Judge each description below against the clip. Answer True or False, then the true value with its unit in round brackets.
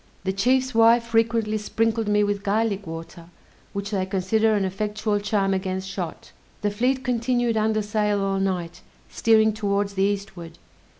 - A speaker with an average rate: True (155 wpm)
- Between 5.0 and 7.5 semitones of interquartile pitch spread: False (2.5 semitones)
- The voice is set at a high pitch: True (205 Hz)